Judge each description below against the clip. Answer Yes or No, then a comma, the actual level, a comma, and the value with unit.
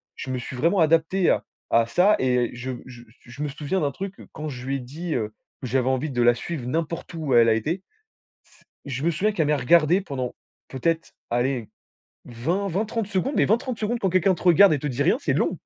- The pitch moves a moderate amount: No, wide, 6.3 semitones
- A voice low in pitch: No, medium, 150 Hz